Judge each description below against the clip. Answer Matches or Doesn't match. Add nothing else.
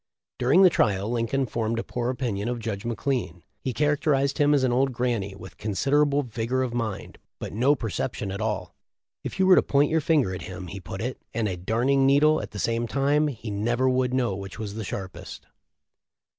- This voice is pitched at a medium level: Doesn't match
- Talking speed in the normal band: Doesn't match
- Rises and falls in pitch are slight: Doesn't match